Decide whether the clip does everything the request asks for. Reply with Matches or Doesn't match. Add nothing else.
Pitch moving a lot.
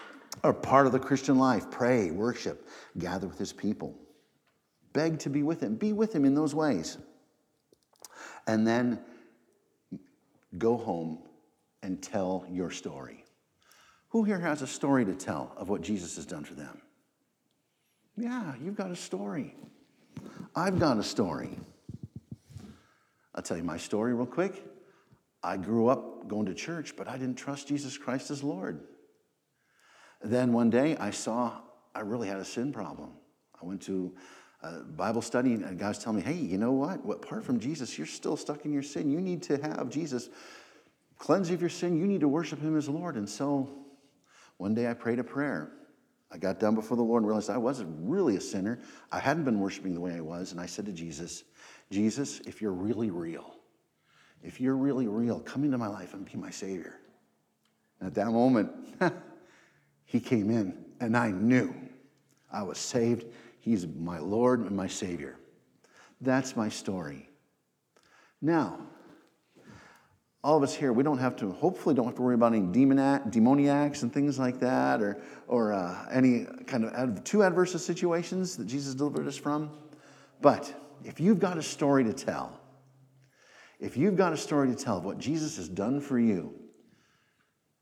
Doesn't match